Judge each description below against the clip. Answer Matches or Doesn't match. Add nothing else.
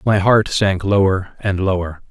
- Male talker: Matches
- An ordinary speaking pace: Matches